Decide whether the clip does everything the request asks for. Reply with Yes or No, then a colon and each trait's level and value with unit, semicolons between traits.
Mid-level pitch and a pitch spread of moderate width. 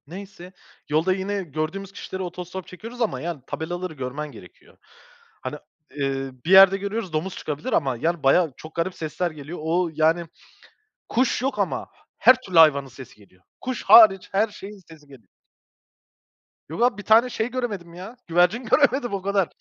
Yes: medium, 180 Hz; average, 4.5 semitones